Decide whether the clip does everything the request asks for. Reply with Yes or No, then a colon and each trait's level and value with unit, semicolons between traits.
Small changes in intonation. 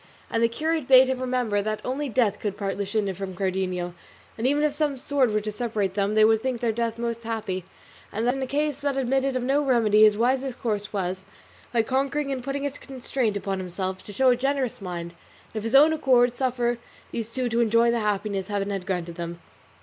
No: average, 4.4 semitones